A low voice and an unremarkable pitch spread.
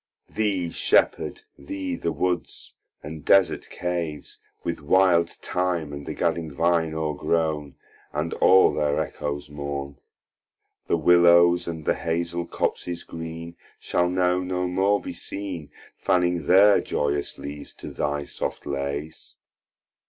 Yes: very low, 85 Hz; average, 3.1 semitones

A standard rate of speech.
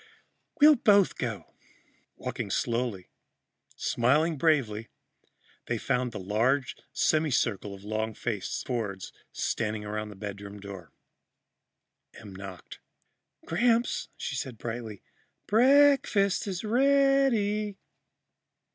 No: slow, 105 wpm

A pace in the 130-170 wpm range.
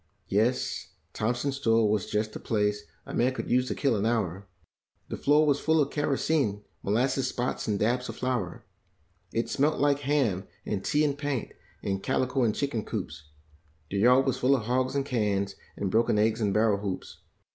No: average, 185 wpm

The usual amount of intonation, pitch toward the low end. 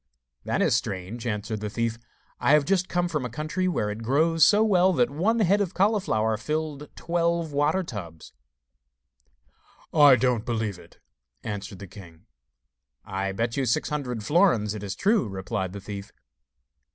No: wide, 8.2 semitones; low, 125 Hz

